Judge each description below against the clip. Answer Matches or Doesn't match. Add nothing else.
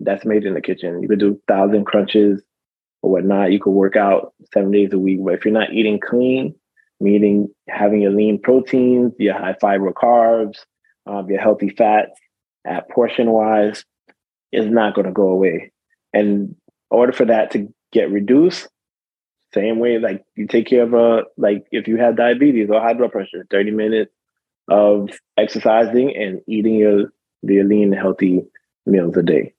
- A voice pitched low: Matches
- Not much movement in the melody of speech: Matches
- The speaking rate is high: Doesn't match